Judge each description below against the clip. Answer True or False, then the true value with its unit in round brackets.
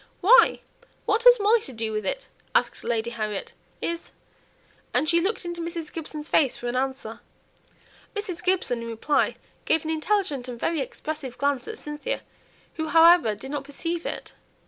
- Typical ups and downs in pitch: False (5.7 semitones)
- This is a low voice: False (310 Hz)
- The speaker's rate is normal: True (170 wpm)